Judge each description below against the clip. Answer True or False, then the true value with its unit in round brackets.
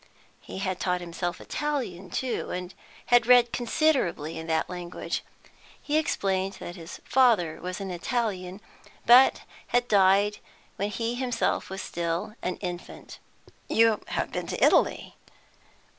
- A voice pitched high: True (195 Hz)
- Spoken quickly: False (135 wpm)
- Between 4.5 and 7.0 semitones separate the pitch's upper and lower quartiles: True (5.2 semitones)